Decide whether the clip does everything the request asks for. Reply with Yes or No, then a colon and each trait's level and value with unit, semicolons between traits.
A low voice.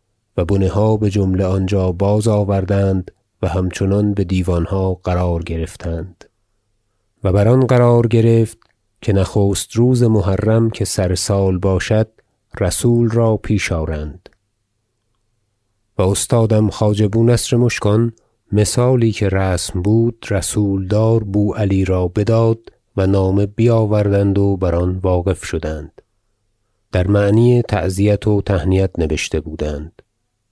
Yes: low, 100 Hz